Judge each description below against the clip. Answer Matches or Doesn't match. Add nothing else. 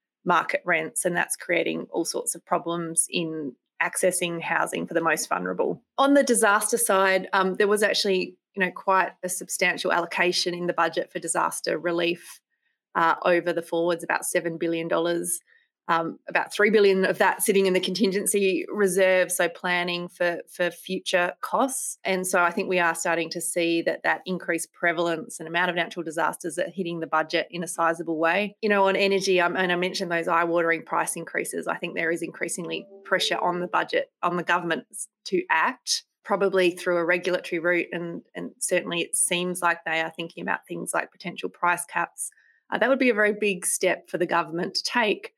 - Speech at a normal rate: Matches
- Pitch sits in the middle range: Matches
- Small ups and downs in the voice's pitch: Matches